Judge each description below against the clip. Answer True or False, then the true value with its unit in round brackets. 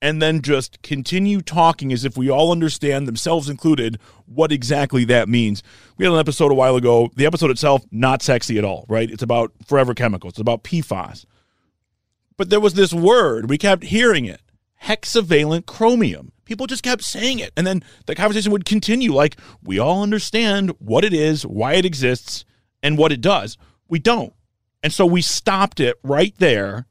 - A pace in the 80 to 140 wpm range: False (185 wpm)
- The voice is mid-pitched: True (145 Hz)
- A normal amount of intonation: False (7.9 semitones)